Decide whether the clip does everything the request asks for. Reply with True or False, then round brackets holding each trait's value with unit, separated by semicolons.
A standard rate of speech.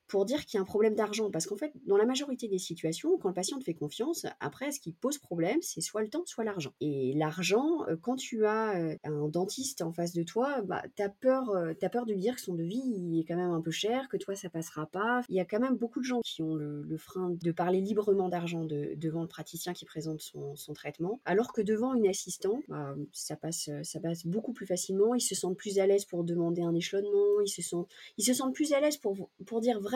False (260 wpm)